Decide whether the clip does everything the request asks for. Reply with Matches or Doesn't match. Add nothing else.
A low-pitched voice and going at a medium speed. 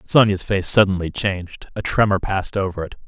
Matches